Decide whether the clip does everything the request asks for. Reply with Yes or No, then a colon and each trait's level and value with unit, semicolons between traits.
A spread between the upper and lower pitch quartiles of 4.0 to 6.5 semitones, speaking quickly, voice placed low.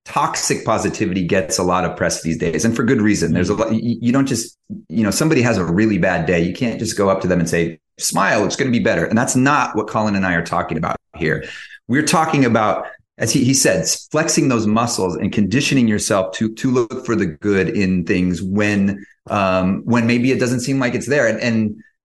Yes: average, 4.5 semitones; fast, 235 wpm; low, 110 Hz